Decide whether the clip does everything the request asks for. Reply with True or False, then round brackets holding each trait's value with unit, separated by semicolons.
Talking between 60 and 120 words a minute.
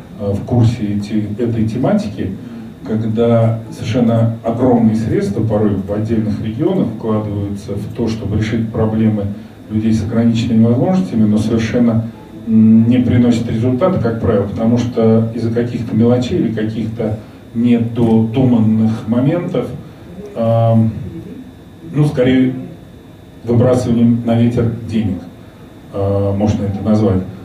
True (110 wpm)